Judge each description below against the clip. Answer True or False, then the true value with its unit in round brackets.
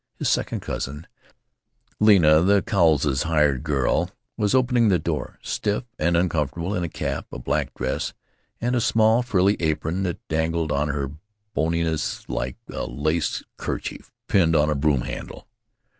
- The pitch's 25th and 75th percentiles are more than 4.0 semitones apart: True (4.7 semitones)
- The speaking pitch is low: True (80 Hz)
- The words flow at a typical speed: True (150 wpm)